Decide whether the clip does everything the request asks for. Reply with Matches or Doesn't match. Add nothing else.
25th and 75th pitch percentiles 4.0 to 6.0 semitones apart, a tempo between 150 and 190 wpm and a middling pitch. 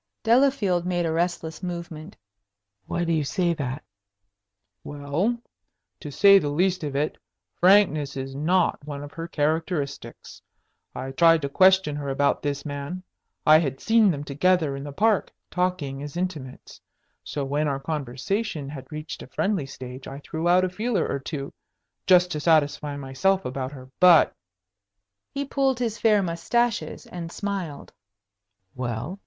Matches